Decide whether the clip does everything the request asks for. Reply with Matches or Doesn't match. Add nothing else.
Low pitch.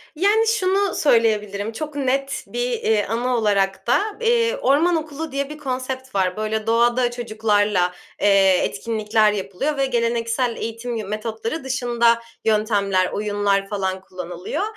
Doesn't match